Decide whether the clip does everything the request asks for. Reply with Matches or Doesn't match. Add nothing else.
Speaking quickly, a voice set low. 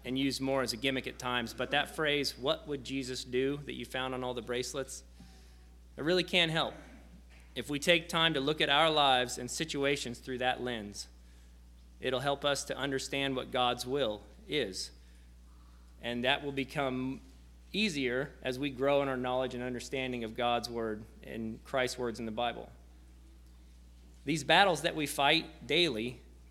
Doesn't match